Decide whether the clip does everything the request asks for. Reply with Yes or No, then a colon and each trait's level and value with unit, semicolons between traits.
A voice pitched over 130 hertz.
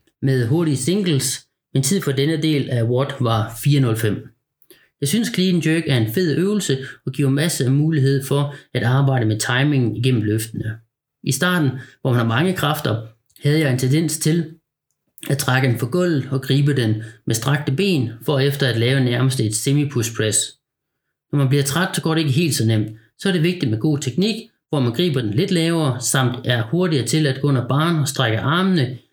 Yes: medium, 140 Hz